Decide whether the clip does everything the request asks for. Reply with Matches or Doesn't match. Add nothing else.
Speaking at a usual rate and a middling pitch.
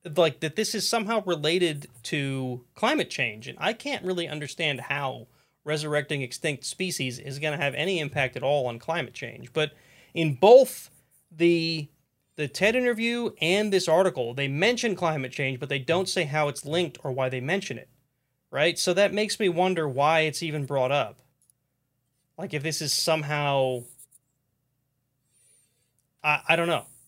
Matches